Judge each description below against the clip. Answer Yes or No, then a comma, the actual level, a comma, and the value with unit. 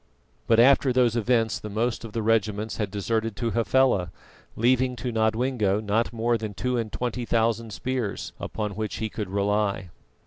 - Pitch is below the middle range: Yes, low, 115 Hz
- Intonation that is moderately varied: No, narrow, 2.2 semitones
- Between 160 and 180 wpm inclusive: Yes, average, 170 wpm